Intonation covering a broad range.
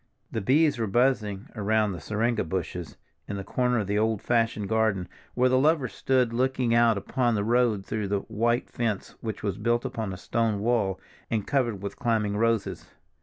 No: average, 2.9 semitones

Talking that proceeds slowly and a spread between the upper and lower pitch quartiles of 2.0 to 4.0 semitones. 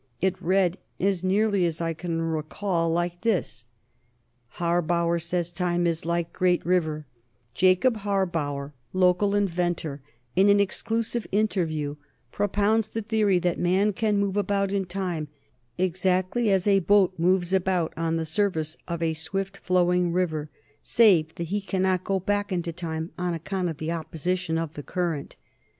No: average, 155 wpm; average, 2.9 semitones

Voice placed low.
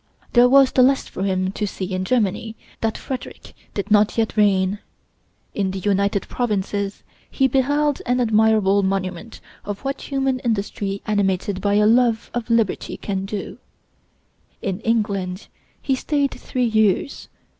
No: high, 210 Hz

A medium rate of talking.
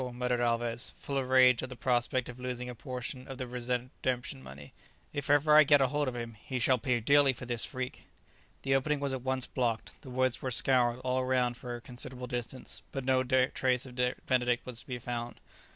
No: fast, 215 wpm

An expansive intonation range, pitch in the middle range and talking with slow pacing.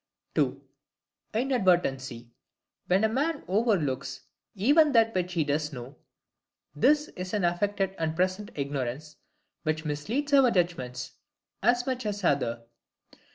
Yes: wide, 7.6 semitones; medium, 180 Hz; slow, 125 wpm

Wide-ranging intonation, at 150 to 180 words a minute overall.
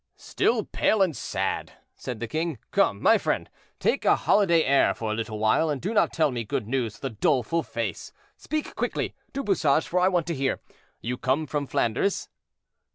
No: wide, 6.3 semitones; average, 190 wpm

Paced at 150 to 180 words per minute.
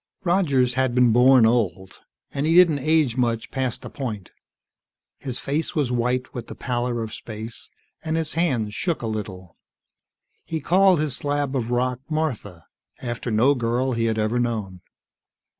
Yes: average, 160 wpm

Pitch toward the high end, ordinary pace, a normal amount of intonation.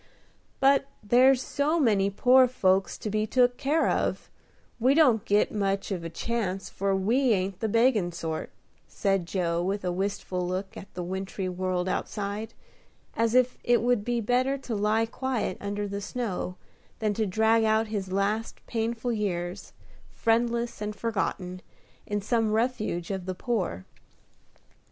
Yes: high, 210 Hz; average, 155 wpm; average, 3.8 semitones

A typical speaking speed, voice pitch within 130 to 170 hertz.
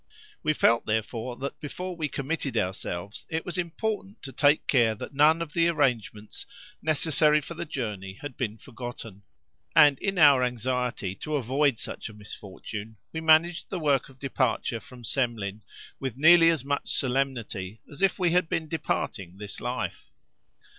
Yes: average, 160 wpm; low, 135 Hz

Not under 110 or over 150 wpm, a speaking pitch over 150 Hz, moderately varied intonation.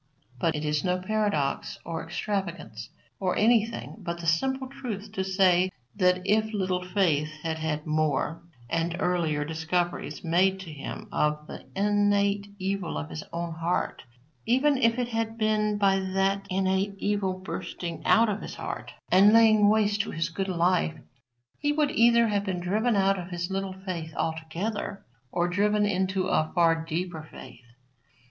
No: average, 160 wpm; high, 190 Hz; average, 3.7 semitones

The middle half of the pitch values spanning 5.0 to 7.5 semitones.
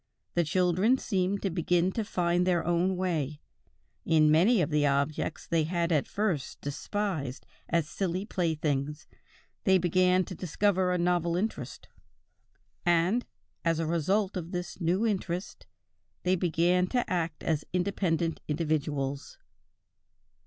No: average, 2.7 semitones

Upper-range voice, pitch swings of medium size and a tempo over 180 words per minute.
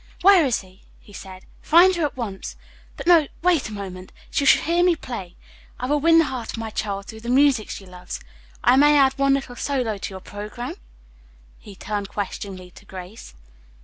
No: high, 235 Hz; wide, 6.6 semitones; average, 200 wpm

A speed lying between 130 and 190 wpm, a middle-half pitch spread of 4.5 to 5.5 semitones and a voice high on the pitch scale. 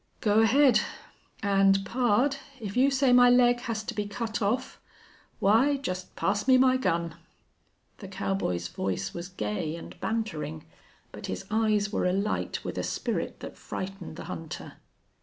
Yes: average, 155 wpm; average, 4.9 semitones; high, 210 Hz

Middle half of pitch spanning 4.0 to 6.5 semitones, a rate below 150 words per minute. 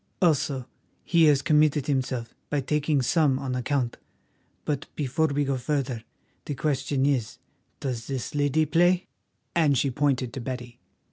No: narrow, 2.6 semitones; average, 140 wpm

